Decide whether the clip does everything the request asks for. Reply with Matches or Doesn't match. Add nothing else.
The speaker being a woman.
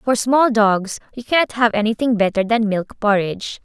Matches